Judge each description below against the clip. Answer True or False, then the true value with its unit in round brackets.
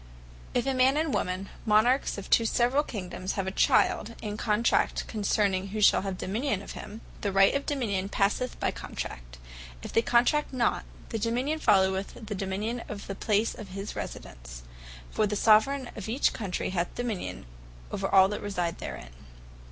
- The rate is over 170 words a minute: True (185 wpm)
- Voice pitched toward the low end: False (210 Hz)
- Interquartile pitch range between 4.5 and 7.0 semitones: False (3.7 semitones)